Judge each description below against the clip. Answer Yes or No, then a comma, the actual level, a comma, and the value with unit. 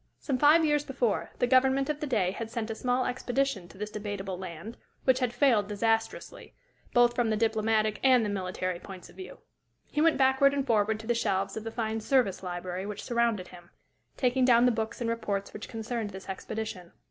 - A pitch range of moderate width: Yes, average, 4.0 semitones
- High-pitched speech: Yes, high, 225 Hz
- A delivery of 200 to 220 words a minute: Yes, fast, 205 wpm